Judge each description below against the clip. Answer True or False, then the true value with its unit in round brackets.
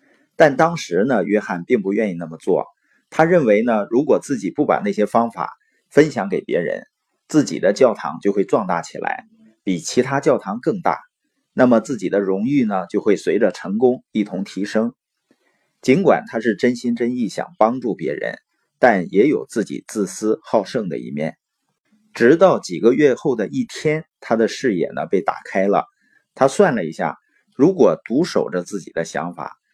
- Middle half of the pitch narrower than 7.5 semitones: True (5.2 semitones)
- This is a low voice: True (110 Hz)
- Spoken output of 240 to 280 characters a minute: True (255 characters per minute)